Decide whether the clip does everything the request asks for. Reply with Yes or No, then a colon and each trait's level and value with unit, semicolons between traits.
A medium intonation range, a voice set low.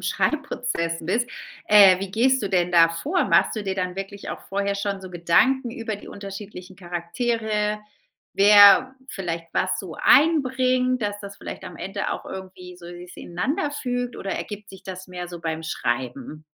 No: average, 4.3 semitones; high, 195 Hz